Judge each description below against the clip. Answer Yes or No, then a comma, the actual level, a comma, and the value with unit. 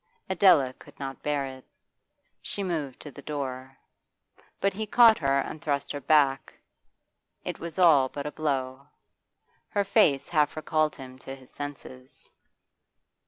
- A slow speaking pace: No, average, 145 wpm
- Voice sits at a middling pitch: Yes, medium, 145 Hz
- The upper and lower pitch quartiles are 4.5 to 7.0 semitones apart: No, average, 2.9 semitones